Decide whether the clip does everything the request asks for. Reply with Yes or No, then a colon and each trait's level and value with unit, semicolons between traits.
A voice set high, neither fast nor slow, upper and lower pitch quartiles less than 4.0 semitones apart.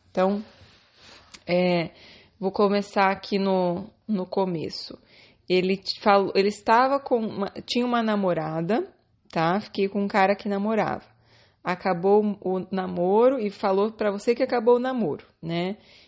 Yes: high, 195 Hz; average, 135 wpm; average, 2.8 semitones